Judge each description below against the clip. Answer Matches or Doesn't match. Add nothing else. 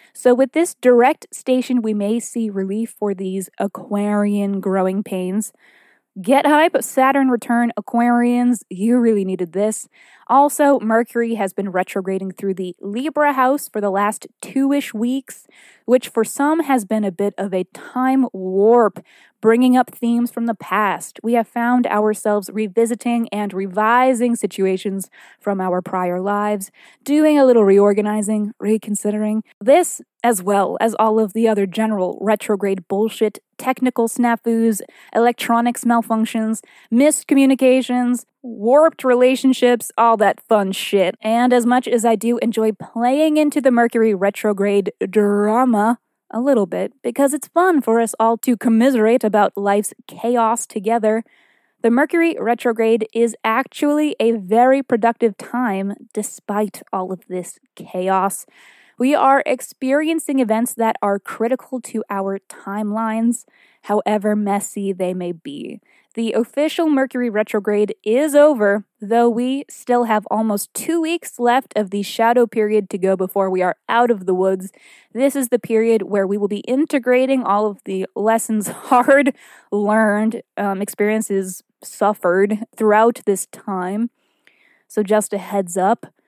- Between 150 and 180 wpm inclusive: Doesn't match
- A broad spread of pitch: Doesn't match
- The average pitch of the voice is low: Doesn't match